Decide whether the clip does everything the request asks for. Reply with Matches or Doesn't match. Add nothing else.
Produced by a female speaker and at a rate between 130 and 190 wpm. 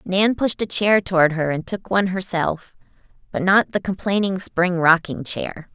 Matches